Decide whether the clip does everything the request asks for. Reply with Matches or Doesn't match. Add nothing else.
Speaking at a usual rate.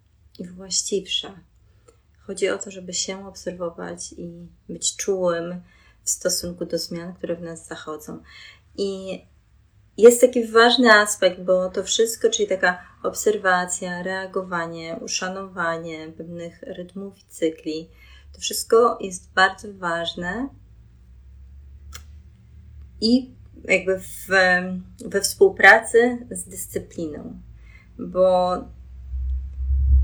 Doesn't match